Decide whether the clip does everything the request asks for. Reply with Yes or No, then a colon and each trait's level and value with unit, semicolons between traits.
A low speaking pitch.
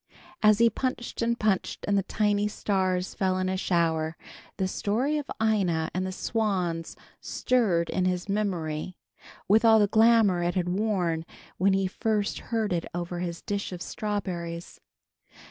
No: high, 190 Hz